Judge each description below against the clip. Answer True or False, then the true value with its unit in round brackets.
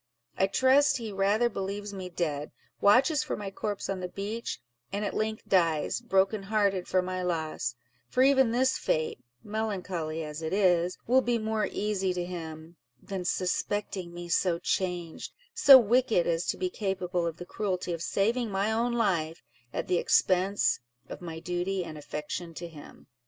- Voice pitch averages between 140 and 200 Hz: True (190 Hz)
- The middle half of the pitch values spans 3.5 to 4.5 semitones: True (3.9 semitones)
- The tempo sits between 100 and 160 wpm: False (170 wpm)